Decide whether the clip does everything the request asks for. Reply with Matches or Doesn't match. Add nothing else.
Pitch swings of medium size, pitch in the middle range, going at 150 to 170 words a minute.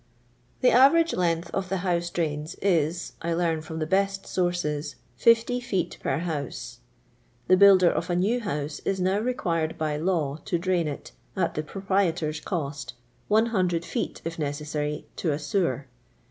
Matches